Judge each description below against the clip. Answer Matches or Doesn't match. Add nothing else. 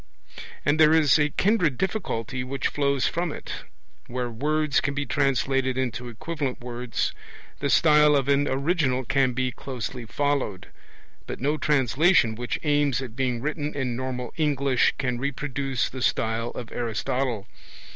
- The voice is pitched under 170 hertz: Matches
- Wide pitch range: Doesn't match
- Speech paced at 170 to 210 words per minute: Doesn't match